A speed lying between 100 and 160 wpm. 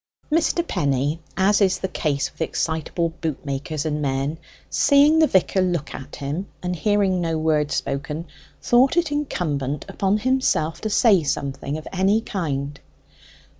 Yes: average, 150 wpm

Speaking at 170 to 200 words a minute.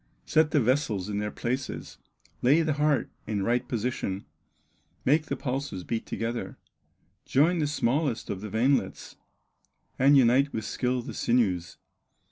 No: average, 140 wpm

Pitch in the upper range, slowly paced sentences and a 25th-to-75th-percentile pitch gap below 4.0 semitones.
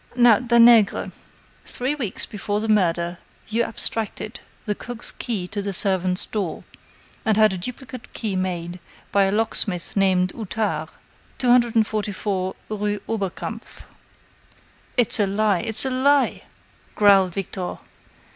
Yes: high, 210 Hz; slow, 125 wpm; average, 3.2 semitones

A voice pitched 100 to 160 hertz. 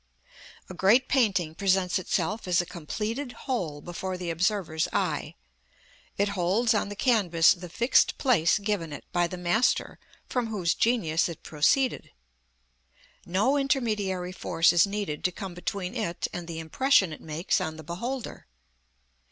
No: medium, 185 Hz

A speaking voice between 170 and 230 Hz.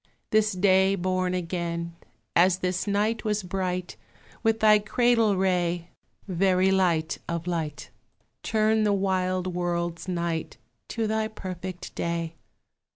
Yes: medium, 185 Hz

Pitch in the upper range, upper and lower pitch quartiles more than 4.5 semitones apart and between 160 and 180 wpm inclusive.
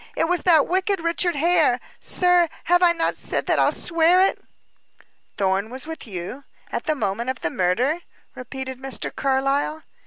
Yes: very high, 295 Hz; average, 5.3 semitones; average, 165 wpm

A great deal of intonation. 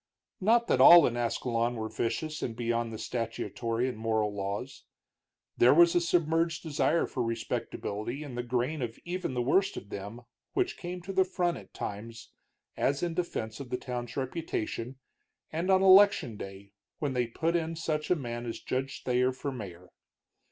Yes: wide, 6.3 semitones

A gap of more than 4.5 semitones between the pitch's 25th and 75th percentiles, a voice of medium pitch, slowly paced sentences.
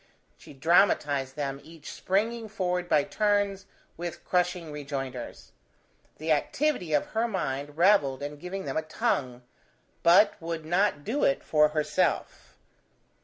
Yes: average, 5.1 semitones; medium, 165 Hz; slow, 130 wpm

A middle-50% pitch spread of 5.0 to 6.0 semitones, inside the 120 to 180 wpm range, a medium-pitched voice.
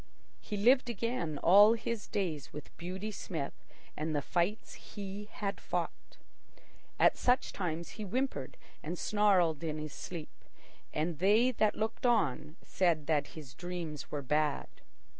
Yes: wide, 5.4 semitones; average, 140 wpm; medium, 180 Hz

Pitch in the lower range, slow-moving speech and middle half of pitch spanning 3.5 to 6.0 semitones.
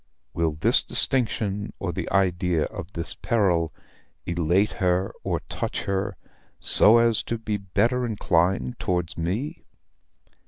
Yes: very low, 95 Hz; slow, 125 wpm; average, 3.9 semitones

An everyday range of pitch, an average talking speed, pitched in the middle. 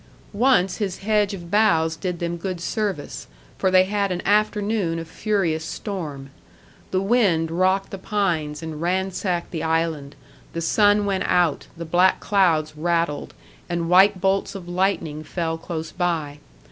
Yes: average, 3.3 semitones; average, 150 wpm; medium, 180 Hz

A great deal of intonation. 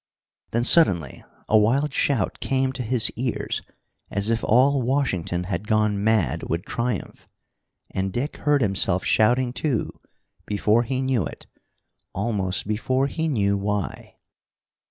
No: average, 4.6 semitones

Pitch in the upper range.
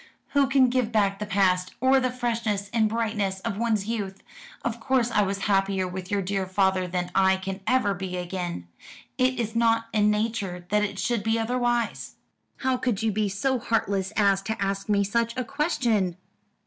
Yes: high, 210 Hz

